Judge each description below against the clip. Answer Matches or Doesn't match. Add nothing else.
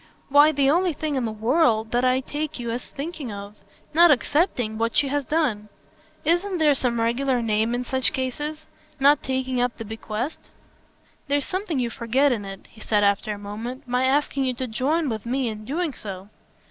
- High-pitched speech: Matches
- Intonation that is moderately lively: Matches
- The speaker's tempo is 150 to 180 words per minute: Doesn't match